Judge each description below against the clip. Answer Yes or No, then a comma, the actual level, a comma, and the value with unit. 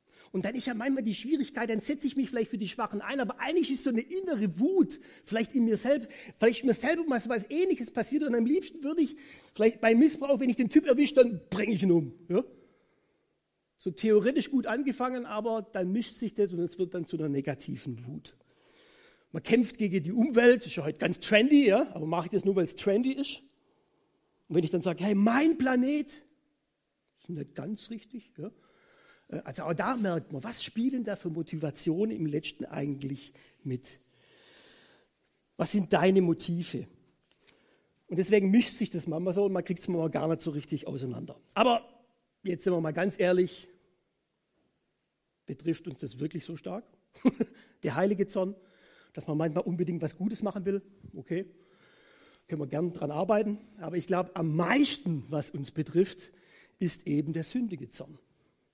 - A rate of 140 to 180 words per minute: No, fast, 190 wpm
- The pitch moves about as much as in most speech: No, wide, 6.6 semitones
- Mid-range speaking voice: No, high, 205 Hz